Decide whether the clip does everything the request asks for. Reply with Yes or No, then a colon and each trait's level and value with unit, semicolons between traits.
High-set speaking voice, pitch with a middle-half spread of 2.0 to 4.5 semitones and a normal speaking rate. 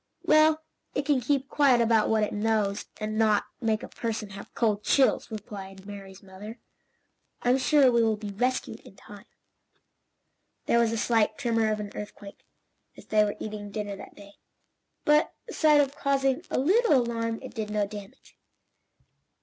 Yes: high, 220 Hz; average, 3.8 semitones; average, 165 wpm